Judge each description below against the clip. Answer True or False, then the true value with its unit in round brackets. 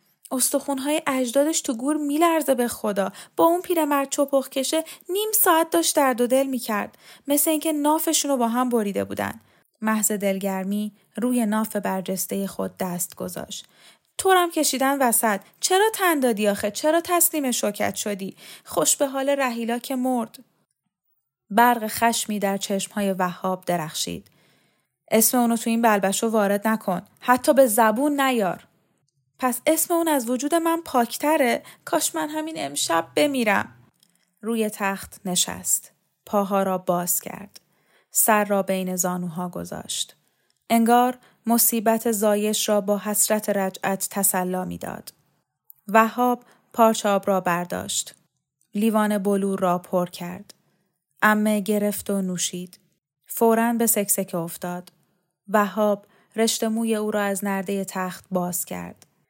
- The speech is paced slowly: False (130 wpm)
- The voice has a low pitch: False (215 Hz)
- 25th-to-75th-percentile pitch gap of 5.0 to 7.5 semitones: True (5.5 semitones)